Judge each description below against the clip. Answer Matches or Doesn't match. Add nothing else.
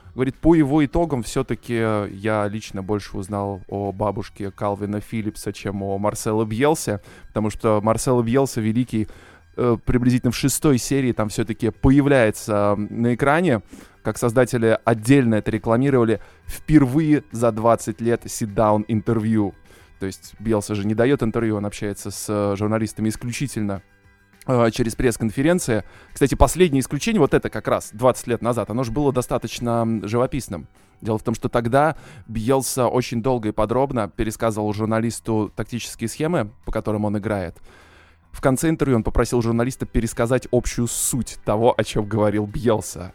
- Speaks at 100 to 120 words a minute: Doesn't match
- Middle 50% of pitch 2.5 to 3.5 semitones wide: Matches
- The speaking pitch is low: Matches